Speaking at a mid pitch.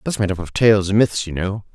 No: low, 100 Hz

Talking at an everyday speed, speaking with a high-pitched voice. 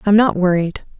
Yes: average, 180 wpm; high, 195 Hz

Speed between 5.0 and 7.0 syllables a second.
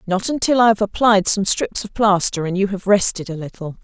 Yes: 5.4 syllables/s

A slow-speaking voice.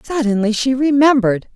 Yes: slow, 115 wpm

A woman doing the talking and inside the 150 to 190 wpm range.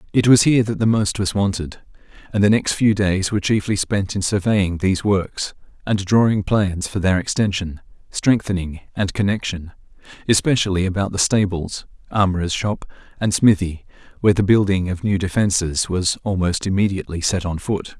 No: male; average, 160 wpm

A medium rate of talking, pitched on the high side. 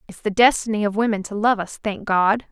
No: fast, 240 wpm; high, 210 Hz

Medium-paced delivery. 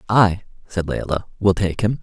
Yes: average, 180 wpm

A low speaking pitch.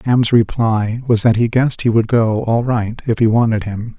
Yes: low, 115 Hz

